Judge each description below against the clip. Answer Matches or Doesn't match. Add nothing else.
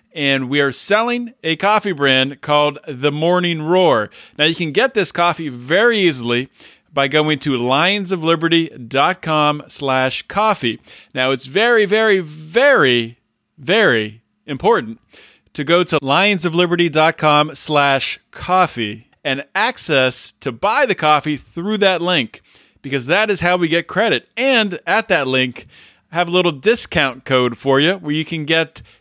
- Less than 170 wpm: Matches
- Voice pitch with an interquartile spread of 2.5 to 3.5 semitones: Doesn't match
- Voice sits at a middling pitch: Matches